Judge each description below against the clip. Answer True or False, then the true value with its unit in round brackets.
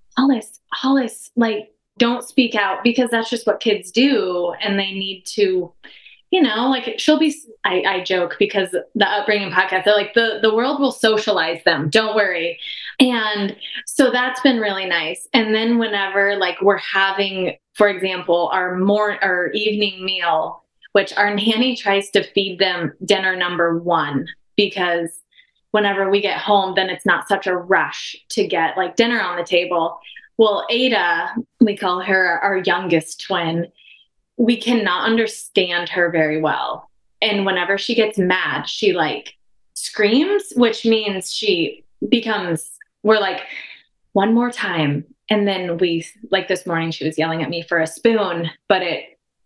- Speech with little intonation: False (4.1 semitones)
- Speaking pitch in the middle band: False (200 Hz)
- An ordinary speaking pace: True (160 wpm)